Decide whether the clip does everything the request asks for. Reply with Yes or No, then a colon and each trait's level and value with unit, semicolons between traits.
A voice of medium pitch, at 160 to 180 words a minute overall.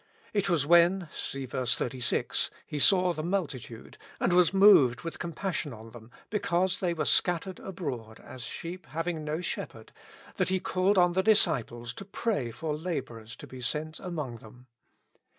Yes: medium, 165 Hz; average, 165 wpm